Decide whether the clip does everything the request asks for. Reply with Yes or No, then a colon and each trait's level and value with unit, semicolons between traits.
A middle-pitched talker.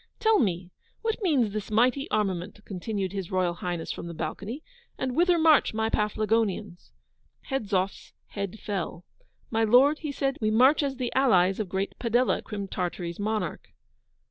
No: high, 215 Hz